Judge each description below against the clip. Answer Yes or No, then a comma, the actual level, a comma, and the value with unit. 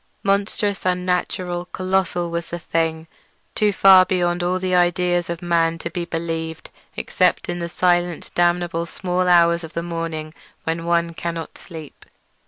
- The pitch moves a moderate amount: No, narrow, 1.3 semitones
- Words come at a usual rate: No, slow, 130 wpm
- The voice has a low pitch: No, medium, 175 Hz